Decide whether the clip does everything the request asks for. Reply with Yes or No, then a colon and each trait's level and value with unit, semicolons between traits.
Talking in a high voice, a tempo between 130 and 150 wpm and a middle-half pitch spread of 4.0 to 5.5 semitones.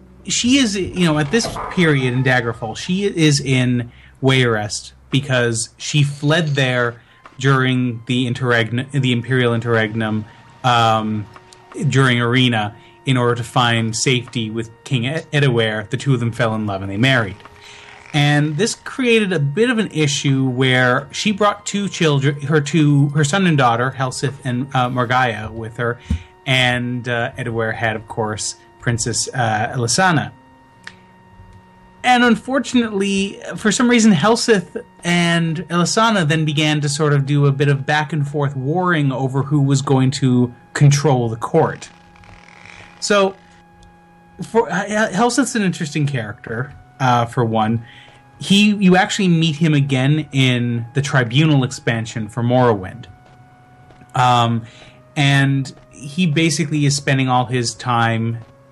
No: low, 130 Hz; average, 140 wpm; average, 4.9 semitones